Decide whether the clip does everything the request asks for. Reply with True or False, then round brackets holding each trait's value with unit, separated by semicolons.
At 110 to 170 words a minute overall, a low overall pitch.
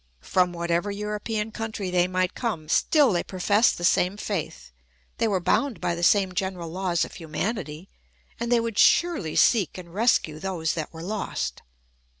False (165 wpm; 185 Hz)